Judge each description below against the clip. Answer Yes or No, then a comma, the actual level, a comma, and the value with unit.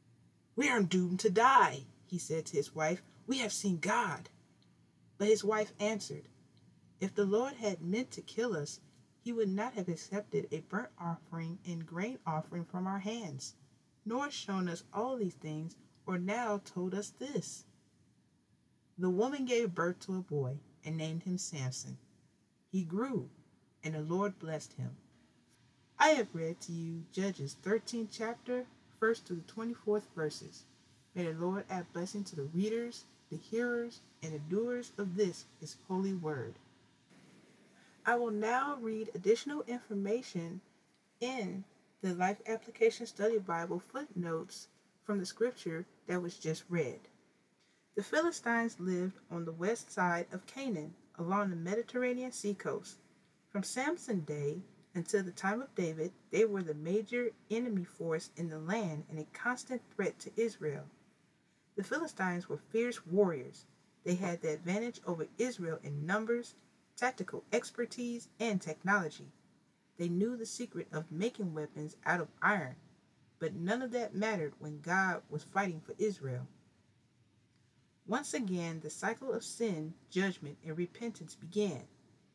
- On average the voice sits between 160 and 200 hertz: Yes, high, 190 Hz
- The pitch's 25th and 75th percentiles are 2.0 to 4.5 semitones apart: No, average, 5.2 semitones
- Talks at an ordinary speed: Yes, average, 150 wpm